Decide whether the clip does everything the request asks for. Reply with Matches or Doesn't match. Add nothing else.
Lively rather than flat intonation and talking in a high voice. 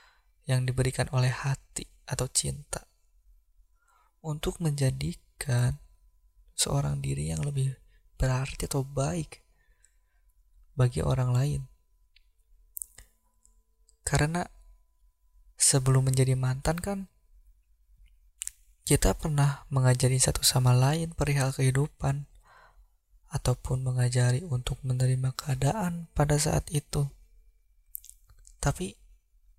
Doesn't match